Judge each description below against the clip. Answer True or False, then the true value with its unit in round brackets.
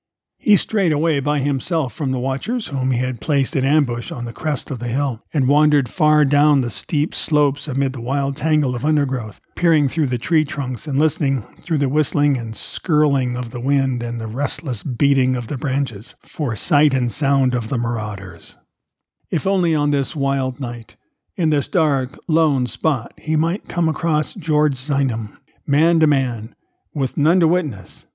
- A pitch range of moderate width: True (3.2 semitones)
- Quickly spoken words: False (185 wpm)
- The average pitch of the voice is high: False (140 Hz)